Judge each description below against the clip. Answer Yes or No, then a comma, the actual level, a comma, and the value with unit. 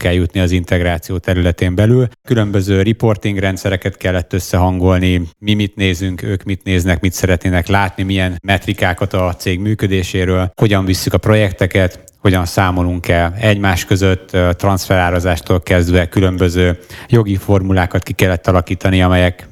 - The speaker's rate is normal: Yes, average, 130 wpm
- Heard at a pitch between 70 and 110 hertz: Yes, very low, 95 Hz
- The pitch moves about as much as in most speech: No, narrow, 1.7 semitones